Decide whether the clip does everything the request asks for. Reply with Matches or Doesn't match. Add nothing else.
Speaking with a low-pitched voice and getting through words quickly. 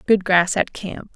Doesn't match